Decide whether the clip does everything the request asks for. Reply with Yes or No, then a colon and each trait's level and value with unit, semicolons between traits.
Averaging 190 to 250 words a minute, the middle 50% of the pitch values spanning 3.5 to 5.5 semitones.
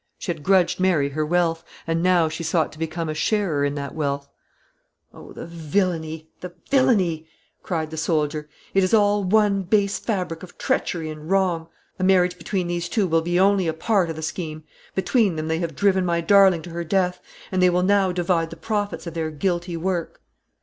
No: average, 200 wpm; average, 2.9 semitones